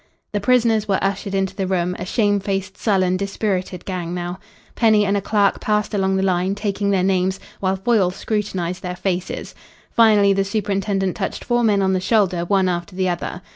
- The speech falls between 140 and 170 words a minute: No, average, 190 wpm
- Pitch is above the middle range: Yes, high, 195 Hz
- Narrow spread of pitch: Yes, narrow, 1.9 semitones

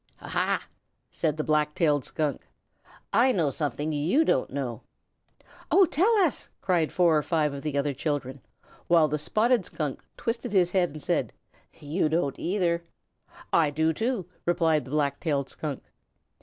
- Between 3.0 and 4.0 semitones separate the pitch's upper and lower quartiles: Yes, average, 3.7 semitones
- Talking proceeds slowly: No, average, 155 wpm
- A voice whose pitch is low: No, medium, 155 Hz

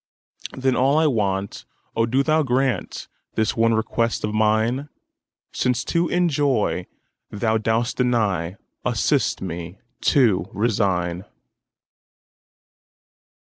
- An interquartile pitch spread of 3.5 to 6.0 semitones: Yes, average, 4.6 semitones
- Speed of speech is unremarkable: No, slow, 85 wpm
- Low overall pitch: Yes, low, 115 Hz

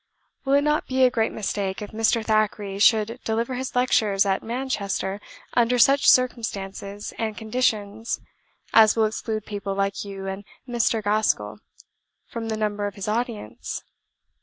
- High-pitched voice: Yes, high, 215 Hz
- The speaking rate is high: No, average, 150 wpm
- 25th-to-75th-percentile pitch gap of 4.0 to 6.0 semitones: No, average, 2.8 semitones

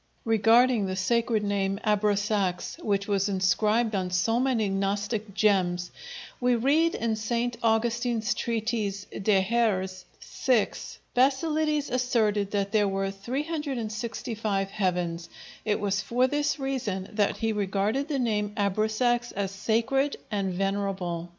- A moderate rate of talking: No, slow, 125 wpm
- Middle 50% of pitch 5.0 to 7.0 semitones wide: No, average, 3.3 semitones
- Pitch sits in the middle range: No, high, 215 Hz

